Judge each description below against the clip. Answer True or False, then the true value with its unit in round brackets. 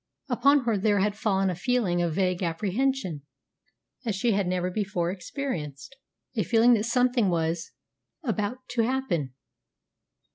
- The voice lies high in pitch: True (205 Hz)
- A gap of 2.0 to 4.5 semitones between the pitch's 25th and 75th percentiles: False (5.5 semitones)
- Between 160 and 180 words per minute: False (145 wpm)